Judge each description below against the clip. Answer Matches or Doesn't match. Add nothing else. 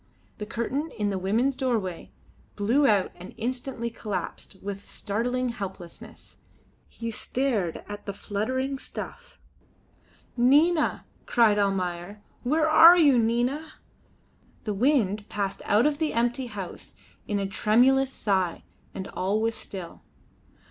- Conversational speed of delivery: Doesn't match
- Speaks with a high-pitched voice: Matches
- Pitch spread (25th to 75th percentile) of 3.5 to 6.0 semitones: Matches